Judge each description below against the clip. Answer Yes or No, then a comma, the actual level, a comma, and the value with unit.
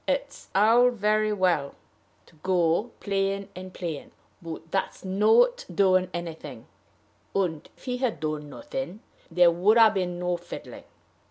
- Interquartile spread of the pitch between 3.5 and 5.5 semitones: Yes, average, 3.9 semitones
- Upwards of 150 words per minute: No, average, 140 wpm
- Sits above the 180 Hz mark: Yes, high, 190 Hz